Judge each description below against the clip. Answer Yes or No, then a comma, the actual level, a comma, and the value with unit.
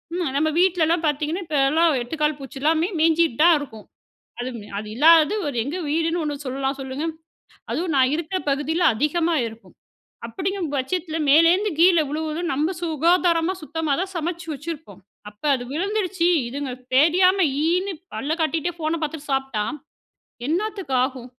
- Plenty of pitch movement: No, average, 3.5 semitones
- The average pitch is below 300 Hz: No, very high, 320 Hz